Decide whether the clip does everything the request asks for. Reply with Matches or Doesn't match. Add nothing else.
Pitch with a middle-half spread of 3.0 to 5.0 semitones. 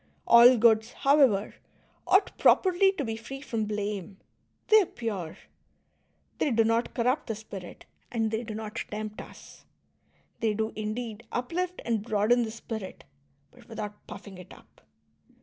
Doesn't match